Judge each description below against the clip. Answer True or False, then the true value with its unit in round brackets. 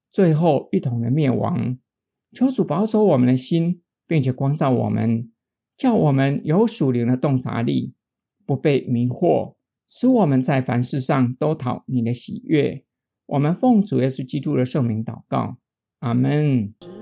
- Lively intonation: False (5.0 semitones)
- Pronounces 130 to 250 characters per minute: True (220 characters per minute)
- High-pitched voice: False (135 Hz)